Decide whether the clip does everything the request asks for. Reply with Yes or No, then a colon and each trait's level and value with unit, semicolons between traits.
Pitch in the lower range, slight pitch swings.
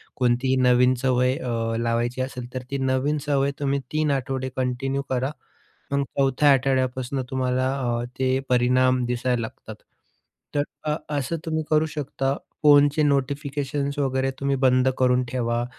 Yes: low, 130 Hz; narrow, 1.7 semitones